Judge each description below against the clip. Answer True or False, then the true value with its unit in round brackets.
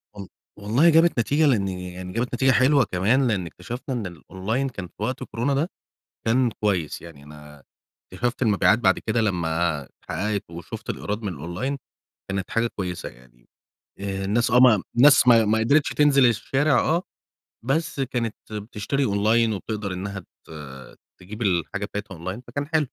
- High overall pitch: False (110 Hz)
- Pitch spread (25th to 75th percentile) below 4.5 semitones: False (5.4 semitones)